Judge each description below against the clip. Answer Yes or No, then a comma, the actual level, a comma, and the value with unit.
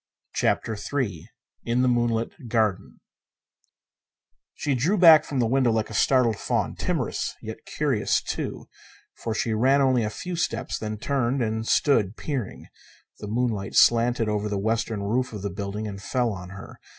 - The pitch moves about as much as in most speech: Yes, average, 3.3 semitones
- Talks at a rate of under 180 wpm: Yes, average, 165 wpm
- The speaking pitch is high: No, low, 115 Hz